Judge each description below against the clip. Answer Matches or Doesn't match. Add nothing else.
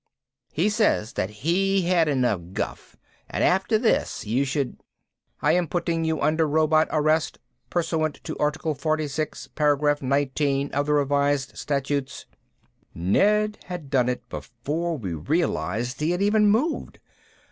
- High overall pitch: Doesn't match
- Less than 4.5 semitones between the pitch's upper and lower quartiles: Matches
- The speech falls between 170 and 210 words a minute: Doesn't match